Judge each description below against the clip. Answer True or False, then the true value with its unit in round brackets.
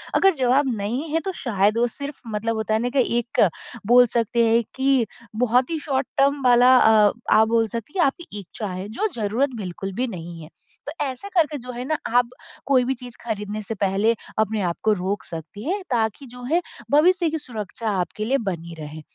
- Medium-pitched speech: False (235 Hz)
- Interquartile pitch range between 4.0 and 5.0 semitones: True (4.5 semitones)